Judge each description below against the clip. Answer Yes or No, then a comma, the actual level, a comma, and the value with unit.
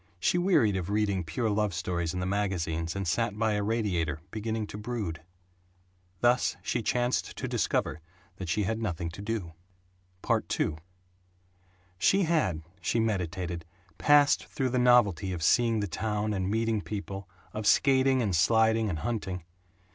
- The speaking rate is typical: Yes, average, 155 wpm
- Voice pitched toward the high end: No, low, 105 Hz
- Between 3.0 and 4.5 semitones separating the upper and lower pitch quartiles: Yes, average, 4.0 semitones